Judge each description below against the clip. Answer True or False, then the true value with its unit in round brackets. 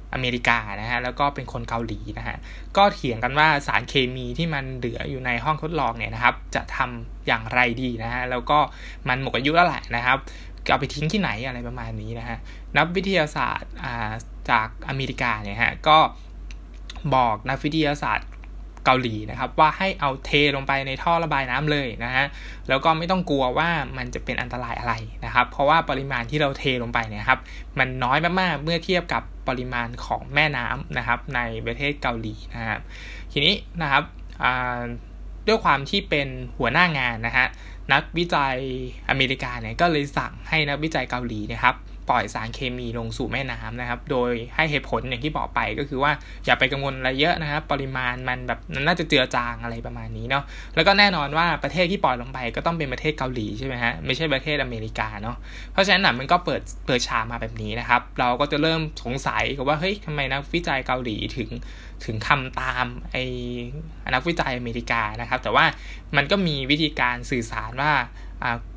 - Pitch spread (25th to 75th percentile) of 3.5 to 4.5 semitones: True (3.8 semitones)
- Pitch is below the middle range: True (130 Hz)